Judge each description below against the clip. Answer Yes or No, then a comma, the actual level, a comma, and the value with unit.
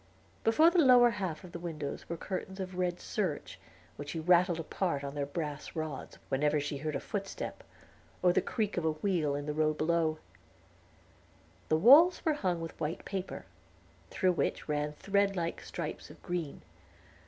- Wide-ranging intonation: No, average, 4.1 semitones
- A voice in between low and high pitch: Yes, medium, 170 Hz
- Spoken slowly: No, average, 175 wpm